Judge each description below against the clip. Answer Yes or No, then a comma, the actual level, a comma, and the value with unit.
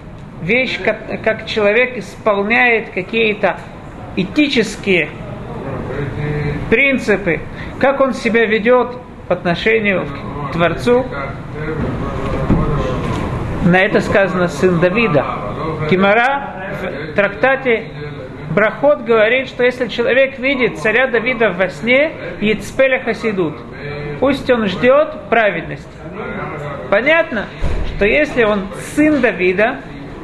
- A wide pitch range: Yes, wide, 6.9 semitones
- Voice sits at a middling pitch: No, high, 210 Hz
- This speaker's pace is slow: Yes, slow, 90 wpm